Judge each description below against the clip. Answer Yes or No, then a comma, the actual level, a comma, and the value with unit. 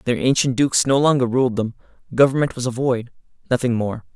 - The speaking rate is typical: Yes, average, 175 wpm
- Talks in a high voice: No, low, 125 Hz